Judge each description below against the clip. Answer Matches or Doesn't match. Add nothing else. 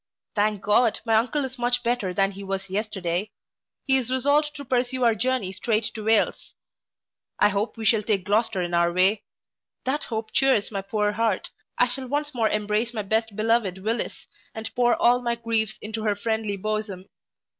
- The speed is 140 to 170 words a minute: Doesn't match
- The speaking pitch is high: Matches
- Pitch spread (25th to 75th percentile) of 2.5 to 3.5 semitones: Matches